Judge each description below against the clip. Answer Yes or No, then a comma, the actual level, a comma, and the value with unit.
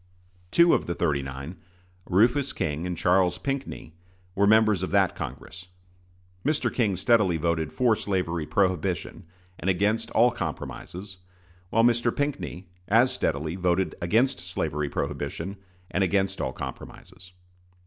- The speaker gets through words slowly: Yes, slow, 130 wpm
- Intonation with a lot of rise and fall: No, average, 4.5 semitones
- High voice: No, very low, 95 Hz